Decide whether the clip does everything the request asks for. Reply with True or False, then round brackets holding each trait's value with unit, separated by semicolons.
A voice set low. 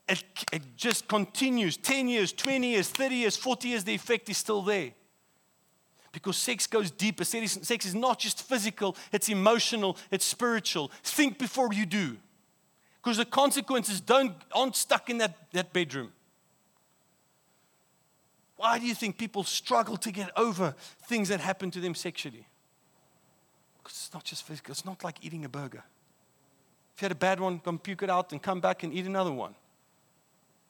False (195 Hz)